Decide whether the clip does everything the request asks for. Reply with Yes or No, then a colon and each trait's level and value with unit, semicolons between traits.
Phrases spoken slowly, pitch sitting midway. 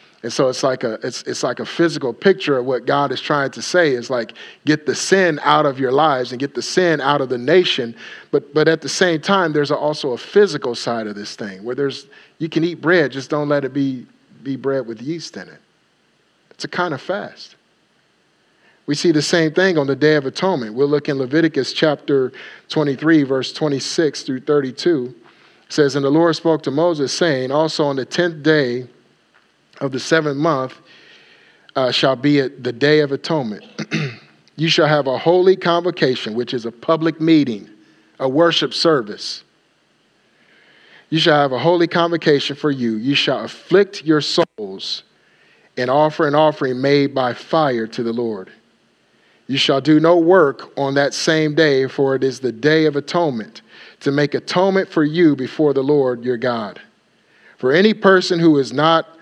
No: average, 190 wpm; medium, 150 Hz